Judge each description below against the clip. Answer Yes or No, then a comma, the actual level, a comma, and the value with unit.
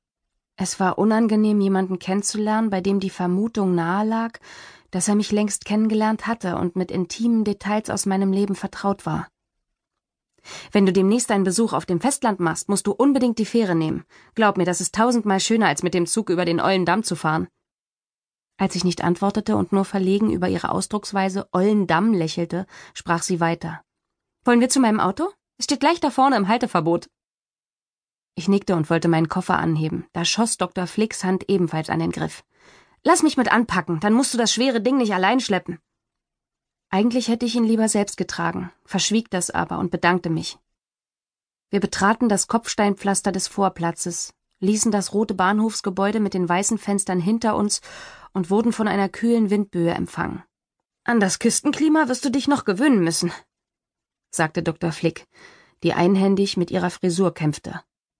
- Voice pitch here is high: Yes, high, 200 Hz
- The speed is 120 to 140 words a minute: No, average, 170 wpm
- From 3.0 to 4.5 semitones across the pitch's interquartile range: Yes, average, 3.6 semitones